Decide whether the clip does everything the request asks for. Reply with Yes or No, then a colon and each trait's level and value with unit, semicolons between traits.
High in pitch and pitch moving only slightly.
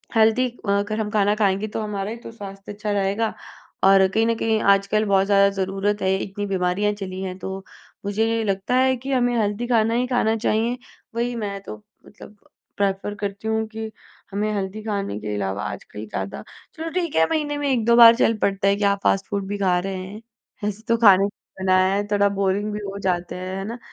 Yes: high, 205 Hz; narrow, 2.3 semitones